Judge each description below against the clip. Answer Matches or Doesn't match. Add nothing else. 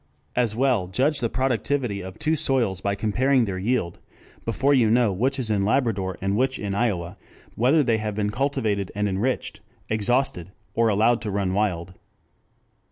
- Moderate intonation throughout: Matches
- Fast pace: Doesn't match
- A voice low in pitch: Matches